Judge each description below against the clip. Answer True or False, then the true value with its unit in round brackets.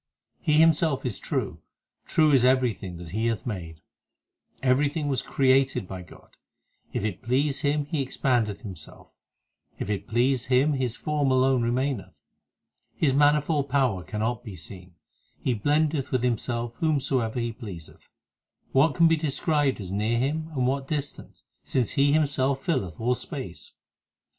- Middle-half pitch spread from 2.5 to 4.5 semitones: True (4.2 semitones)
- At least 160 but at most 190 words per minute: False (150 wpm)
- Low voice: True (130 Hz)